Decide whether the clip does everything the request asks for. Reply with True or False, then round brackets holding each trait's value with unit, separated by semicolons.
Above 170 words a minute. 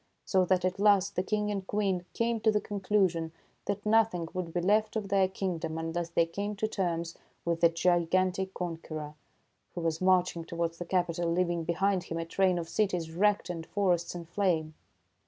True (190 wpm)